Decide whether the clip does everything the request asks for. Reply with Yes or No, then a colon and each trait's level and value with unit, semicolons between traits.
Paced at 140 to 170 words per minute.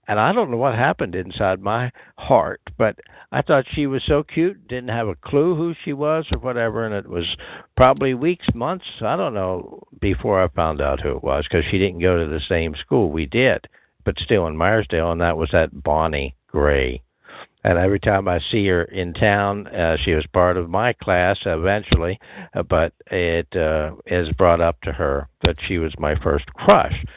No: average, 200 wpm